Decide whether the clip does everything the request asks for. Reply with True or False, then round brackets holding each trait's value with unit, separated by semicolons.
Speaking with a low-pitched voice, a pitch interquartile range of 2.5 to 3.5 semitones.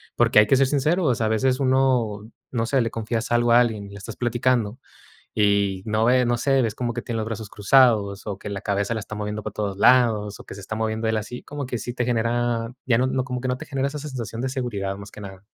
True (115 Hz; 3.2 semitones)